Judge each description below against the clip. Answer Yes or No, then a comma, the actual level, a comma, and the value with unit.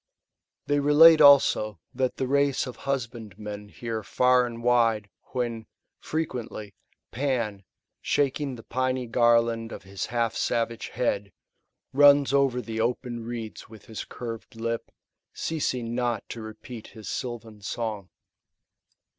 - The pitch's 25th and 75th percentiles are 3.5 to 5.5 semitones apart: No, narrow, 2.6 semitones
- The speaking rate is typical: No, slow, 125 wpm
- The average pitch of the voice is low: Yes, low, 120 Hz